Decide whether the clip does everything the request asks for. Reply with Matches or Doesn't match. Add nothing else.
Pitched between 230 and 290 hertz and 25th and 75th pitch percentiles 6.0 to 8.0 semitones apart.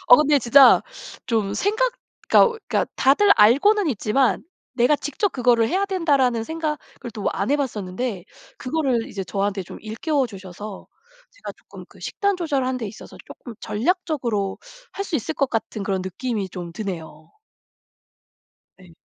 Matches